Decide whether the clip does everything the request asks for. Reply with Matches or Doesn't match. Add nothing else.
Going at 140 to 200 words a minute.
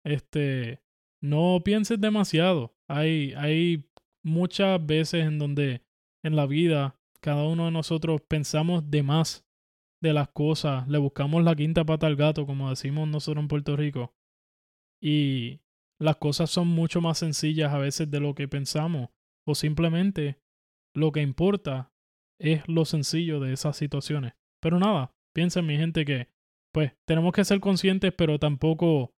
Matches